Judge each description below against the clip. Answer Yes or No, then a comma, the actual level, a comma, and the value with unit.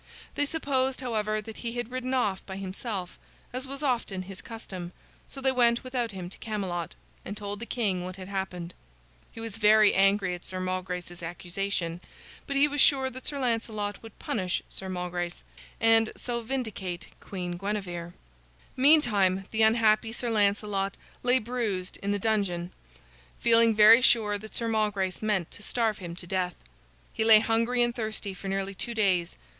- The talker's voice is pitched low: No, high, 210 Hz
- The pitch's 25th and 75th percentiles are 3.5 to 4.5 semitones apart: Yes, average, 3.8 semitones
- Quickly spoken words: No, average, 170 wpm